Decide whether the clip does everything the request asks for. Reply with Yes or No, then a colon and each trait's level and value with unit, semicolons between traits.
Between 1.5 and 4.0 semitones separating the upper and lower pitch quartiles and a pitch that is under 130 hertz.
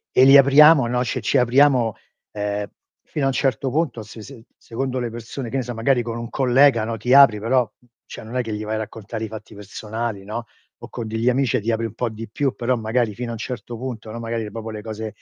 Yes: narrow, 2.6 semitones; low, 115 Hz